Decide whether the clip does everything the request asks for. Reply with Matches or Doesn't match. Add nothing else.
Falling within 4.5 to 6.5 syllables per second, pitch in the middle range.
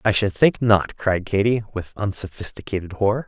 Doesn't match